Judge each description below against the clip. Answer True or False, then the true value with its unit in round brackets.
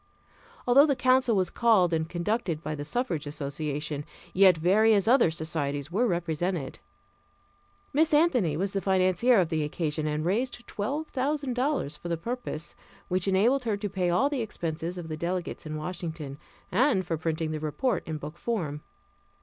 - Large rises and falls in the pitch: True (6.8 semitones)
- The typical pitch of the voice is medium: True (180 Hz)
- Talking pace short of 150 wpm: False (165 wpm)